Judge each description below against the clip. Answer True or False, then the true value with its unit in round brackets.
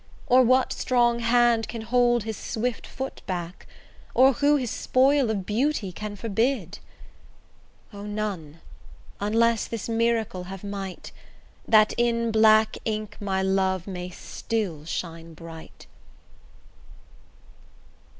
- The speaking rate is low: True (115 wpm)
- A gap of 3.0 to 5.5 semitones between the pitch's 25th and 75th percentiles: True (3.9 semitones)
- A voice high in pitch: True (220 Hz)